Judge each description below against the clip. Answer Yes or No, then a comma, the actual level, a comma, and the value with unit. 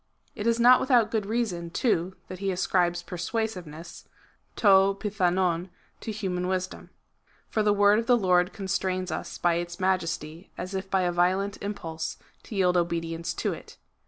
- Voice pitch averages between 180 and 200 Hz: Yes, medium, 185 Hz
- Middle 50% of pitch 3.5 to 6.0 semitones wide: No, average, 2.8 semitones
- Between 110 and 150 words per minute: No, average, 160 wpm